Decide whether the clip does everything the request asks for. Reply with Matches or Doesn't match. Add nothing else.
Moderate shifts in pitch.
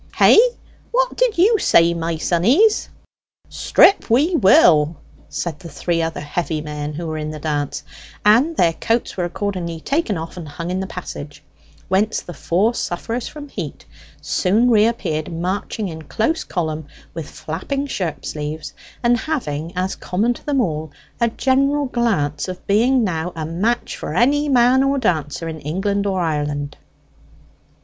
Doesn't match